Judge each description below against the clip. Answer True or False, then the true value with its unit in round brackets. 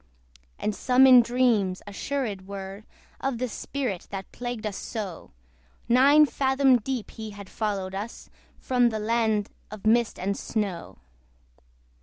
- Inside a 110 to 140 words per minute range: True (135 wpm)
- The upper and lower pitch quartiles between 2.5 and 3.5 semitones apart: False (3.9 semitones)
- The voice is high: True (220 Hz)